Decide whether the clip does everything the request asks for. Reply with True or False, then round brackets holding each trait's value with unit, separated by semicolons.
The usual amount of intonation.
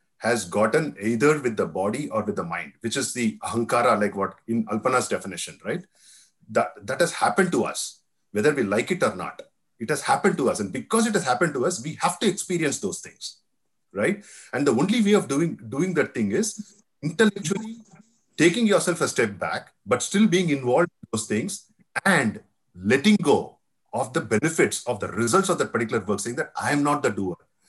False (8.6 semitones)